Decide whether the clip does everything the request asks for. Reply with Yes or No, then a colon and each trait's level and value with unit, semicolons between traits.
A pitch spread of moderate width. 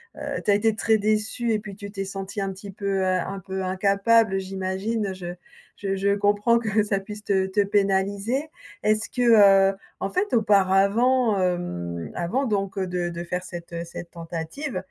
No: narrow, 2.2 semitones